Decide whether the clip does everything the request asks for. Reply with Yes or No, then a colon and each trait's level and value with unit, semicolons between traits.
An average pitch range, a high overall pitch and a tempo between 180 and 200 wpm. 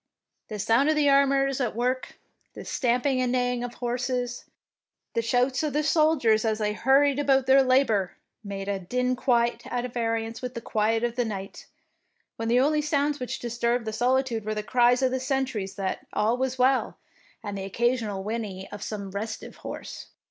Yes: average, 3.1 semitones; high, 245 Hz; average, 185 wpm